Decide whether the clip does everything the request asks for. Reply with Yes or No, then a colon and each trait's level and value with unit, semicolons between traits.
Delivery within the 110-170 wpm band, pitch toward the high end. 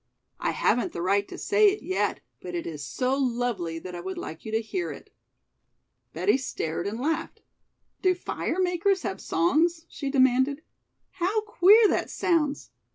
Yes: average, 165 wpm; very high, 275 Hz